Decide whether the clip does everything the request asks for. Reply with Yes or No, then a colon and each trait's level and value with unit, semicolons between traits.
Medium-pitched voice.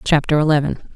Yes: medium, 150 Hz